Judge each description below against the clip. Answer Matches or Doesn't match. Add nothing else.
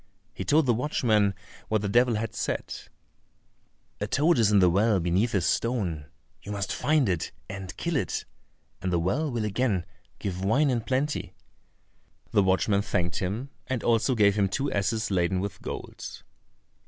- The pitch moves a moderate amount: Matches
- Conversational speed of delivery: Matches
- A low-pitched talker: Matches